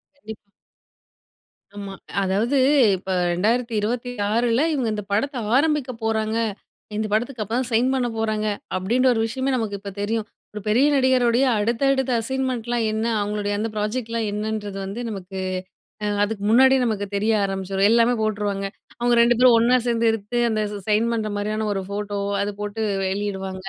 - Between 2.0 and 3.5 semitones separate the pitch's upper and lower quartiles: Yes, average, 2.8 semitones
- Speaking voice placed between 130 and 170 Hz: No, high, 220 Hz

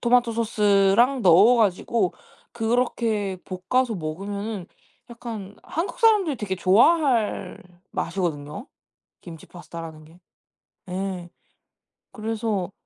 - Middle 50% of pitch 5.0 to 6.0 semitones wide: No, average, 4.3 semitones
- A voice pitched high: Yes, high, 210 Hz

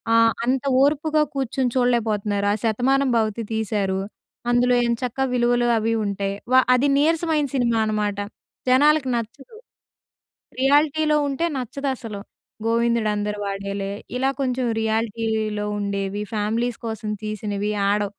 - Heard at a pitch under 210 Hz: No, high, 230 Hz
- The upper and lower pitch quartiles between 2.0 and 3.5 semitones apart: No, average, 3.9 semitones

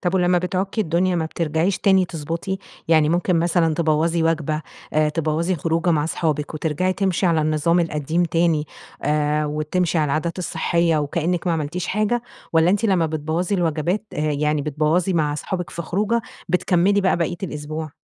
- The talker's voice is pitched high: No, medium, 165 Hz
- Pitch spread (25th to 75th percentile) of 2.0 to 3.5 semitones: Yes, average, 2.7 semitones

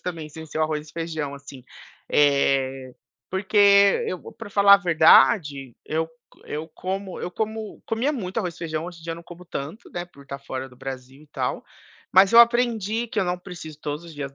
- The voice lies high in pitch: No, medium, 165 Hz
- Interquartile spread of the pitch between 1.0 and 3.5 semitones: No, wide, 5.4 semitones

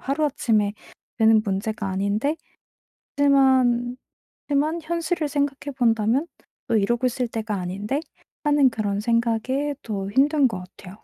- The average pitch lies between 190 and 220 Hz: No, high, 240 Hz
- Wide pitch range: No, average, 5.0 semitones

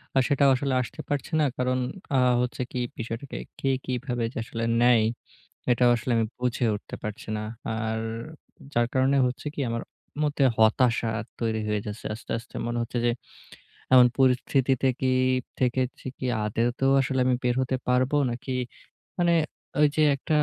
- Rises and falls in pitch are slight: Yes, narrow, 2.3 semitones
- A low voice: Yes, low, 125 Hz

